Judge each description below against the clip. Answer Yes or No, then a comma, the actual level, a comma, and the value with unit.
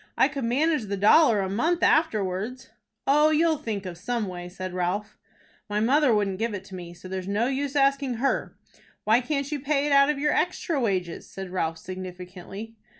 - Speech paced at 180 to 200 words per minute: Yes, average, 195 wpm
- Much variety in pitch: Yes, wide, 6.9 semitones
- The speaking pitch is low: No, high, 225 Hz